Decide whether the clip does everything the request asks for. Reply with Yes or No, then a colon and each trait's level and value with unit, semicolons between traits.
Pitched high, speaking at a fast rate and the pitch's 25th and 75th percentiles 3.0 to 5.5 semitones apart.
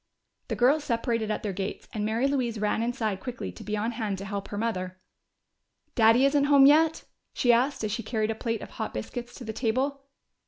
Yes: high, 230 Hz; fast, 210 wpm; average, 3.4 semitones